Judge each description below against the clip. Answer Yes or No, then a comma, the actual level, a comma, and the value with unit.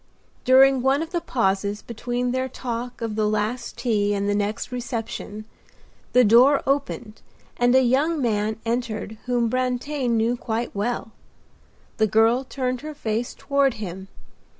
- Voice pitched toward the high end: Yes, high, 240 Hz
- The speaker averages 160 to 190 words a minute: No, average, 150 wpm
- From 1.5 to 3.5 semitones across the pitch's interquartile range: Yes, average, 3.0 semitones